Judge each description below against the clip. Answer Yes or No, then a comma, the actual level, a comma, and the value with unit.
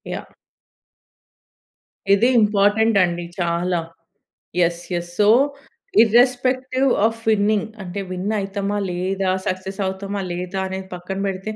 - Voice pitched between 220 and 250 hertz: No, high, 195 Hz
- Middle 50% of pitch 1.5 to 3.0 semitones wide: Yes, average, 2.7 semitones